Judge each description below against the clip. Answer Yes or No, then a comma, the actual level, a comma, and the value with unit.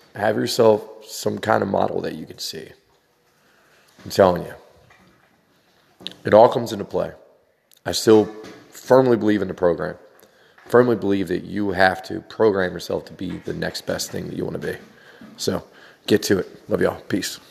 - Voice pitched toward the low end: Yes, low, 105 Hz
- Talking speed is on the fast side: No, average, 175 wpm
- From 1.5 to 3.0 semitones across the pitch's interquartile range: Yes, average, 2.7 semitones